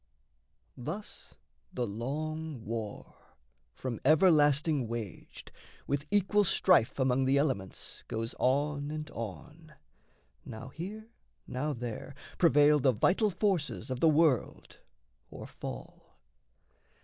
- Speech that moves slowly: Yes, slow, 105 wpm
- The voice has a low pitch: No, medium, 145 Hz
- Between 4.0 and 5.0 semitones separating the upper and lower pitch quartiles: Yes, average, 4.5 semitones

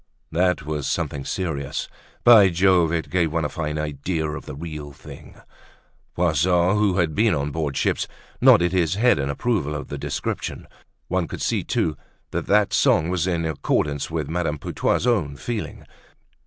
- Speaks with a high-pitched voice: No, very low, 80 Hz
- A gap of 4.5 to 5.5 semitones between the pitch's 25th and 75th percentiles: No, average, 3.6 semitones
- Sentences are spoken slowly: No, average, 170 wpm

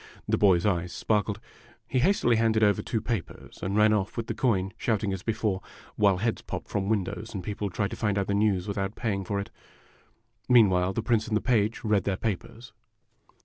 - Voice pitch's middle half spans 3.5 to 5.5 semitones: No, narrow, 2.4 semitones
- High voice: No, low, 105 Hz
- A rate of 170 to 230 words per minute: Yes, average, 200 wpm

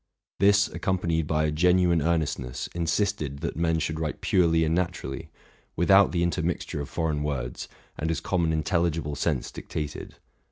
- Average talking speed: Yes, average, 155 wpm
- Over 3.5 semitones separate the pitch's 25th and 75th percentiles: No, narrow, 2.5 semitones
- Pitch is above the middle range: No, very low, 80 Hz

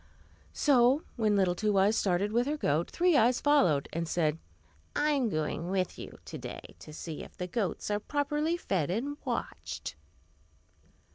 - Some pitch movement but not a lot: No, wide, 8.2 semitones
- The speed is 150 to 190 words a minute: Yes, average, 165 wpm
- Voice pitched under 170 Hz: No, high, 210 Hz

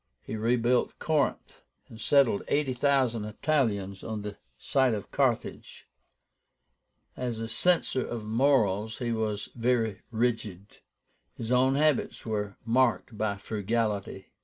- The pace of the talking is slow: Yes, slow, 120 wpm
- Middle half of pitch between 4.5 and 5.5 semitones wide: No, average, 3.2 semitones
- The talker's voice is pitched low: Yes, low, 115 Hz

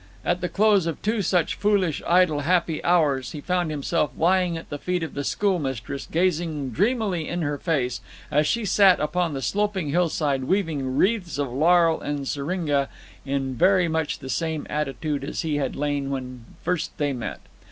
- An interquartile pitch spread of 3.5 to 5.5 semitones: Yes, average, 4.1 semitones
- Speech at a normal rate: Yes, average, 175 wpm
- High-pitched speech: No, medium, 160 Hz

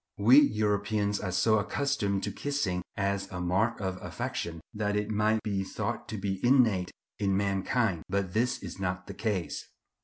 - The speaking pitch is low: Yes, low, 100 Hz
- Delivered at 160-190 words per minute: Yes, average, 165 wpm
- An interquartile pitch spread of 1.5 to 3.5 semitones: Yes, narrow, 2.4 semitones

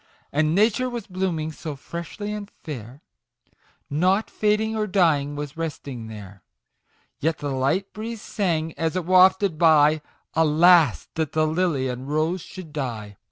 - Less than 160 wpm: Yes, average, 150 wpm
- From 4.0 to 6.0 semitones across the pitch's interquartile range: Yes, average, 4.3 semitones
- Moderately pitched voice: Yes, medium, 160 Hz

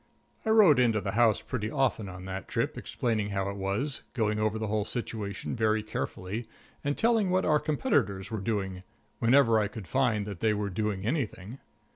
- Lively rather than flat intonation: No, average, 4.0 semitones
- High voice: No, low, 110 Hz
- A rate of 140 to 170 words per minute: No, average, 190 wpm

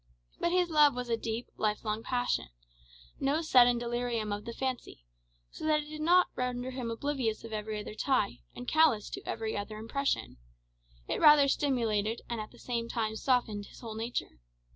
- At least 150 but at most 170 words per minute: No, average, 185 wpm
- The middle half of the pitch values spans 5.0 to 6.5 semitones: No, average, 3.8 semitones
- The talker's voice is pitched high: Yes, high, 240 Hz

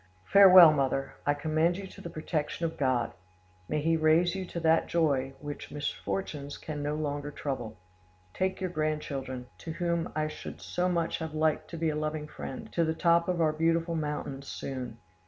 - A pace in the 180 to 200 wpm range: Yes, average, 185 wpm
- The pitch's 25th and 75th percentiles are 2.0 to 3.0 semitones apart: Yes, narrow, 2.6 semitones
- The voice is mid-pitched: Yes, medium, 155 Hz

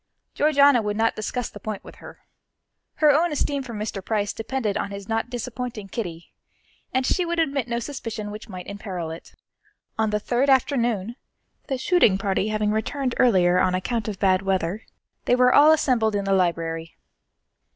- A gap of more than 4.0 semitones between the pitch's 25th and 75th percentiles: Yes, average, 4.6 semitones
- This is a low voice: No, high, 220 Hz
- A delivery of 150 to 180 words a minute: Yes, average, 175 wpm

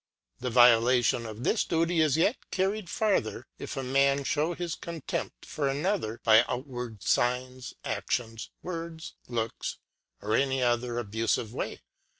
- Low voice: Yes, low, 130 Hz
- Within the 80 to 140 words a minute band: No, average, 155 wpm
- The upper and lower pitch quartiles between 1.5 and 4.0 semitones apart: No, average, 5.3 semitones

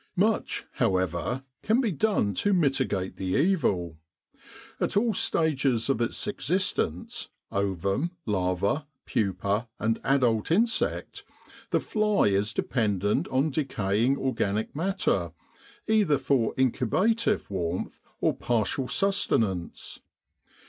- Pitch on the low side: Yes, low, 120 Hz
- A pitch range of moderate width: No, wide, 9.0 semitones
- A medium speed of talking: No, slow, 105 wpm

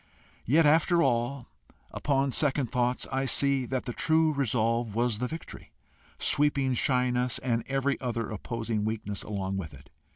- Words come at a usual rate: Yes, average, 150 wpm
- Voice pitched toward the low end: Yes, low, 125 Hz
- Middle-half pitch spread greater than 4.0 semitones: No, average, 3.3 semitones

